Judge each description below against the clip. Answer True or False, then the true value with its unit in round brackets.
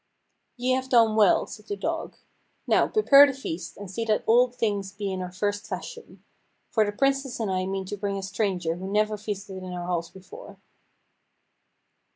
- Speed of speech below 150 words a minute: False (190 wpm)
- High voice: True (205 Hz)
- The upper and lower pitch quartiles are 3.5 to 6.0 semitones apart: True (4.0 semitones)